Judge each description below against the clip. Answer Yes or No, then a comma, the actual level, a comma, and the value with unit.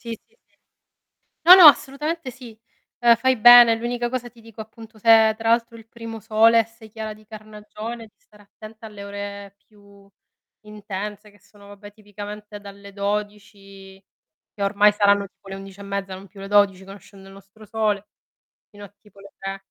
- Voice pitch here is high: Yes, high, 210 Hz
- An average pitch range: No, narrow, 2.1 semitones